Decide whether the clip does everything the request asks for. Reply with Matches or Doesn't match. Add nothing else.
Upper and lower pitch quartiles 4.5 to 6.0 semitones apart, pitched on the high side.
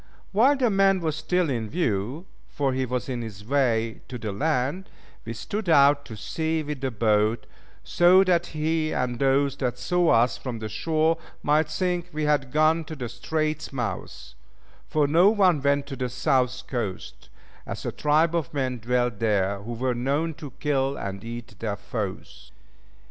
Doesn't match